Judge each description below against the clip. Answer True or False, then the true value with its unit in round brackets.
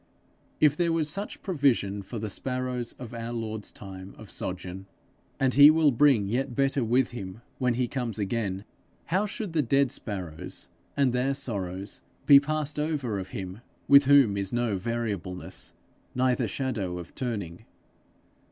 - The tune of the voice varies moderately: False (5.7 semitones)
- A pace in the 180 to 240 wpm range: False (155 wpm)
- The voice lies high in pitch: False (120 Hz)